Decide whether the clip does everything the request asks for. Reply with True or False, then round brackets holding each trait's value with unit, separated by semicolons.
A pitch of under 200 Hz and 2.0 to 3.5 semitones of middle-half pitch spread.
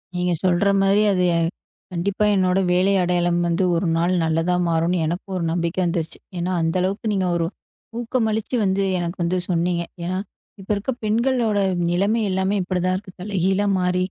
True (185 Hz; 2.4 semitones)